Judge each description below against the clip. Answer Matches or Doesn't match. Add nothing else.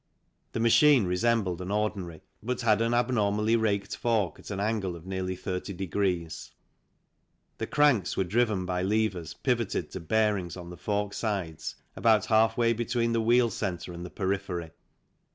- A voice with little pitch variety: Doesn't match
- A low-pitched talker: Matches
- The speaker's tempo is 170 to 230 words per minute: Doesn't match